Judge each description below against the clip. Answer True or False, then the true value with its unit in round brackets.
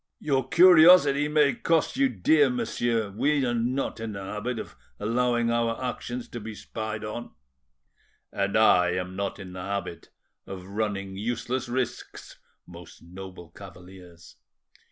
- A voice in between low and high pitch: False (115 Hz)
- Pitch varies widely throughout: False (4.7 semitones)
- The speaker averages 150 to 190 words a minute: False (140 wpm)